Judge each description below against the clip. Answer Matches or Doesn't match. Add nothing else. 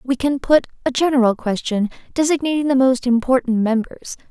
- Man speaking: Doesn't match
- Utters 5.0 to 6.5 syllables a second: Matches